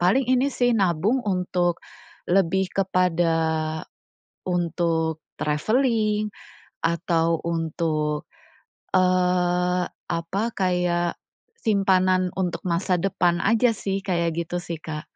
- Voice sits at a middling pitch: Yes, medium, 180 Hz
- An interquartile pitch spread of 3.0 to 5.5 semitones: No, narrow, 2.6 semitones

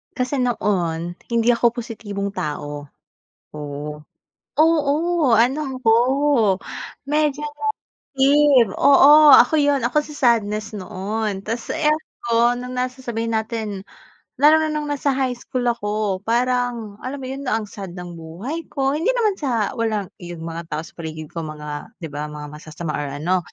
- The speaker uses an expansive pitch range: Yes, wide, 7.3 semitones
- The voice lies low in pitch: No, high, 230 Hz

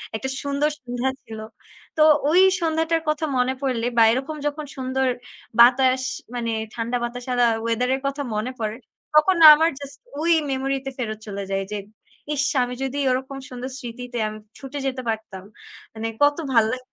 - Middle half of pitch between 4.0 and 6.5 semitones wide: No, average, 3.1 semitones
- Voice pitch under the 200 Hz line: No, very high, 255 Hz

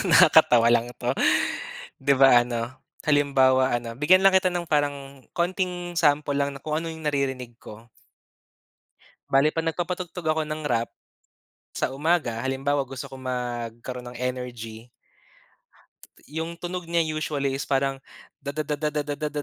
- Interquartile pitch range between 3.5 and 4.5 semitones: Yes, average, 3.9 semitones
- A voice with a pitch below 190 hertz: Yes, medium, 140 Hz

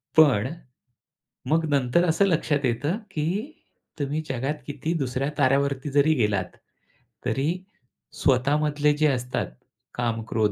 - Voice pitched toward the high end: No, medium, 140 Hz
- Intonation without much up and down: No, average, 3.2 semitones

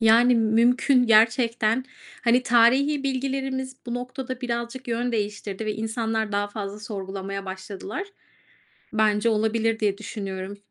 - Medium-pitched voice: No, high, 225 Hz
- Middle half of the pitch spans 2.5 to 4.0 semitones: Yes, average, 3.0 semitones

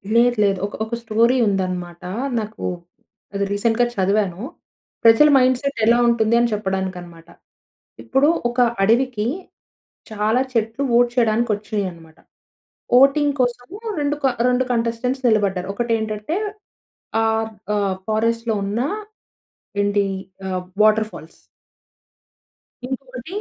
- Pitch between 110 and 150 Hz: No, high, 225 Hz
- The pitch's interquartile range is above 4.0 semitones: No, average, 3.3 semitones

